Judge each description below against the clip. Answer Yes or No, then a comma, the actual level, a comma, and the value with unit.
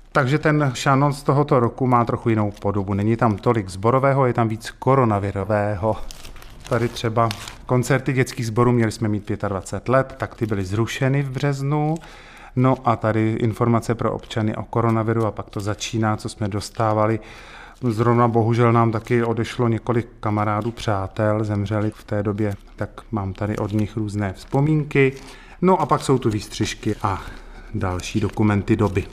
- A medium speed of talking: Yes, average, 160 wpm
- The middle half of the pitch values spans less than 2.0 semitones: No, average, 2.7 semitones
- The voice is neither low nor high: No, low, 115 Hz